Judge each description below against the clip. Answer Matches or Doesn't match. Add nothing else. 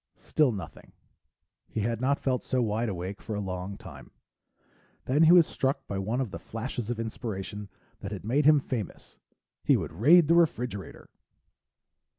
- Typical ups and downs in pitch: Matches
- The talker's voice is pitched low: Matches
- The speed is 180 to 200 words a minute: Doesn't match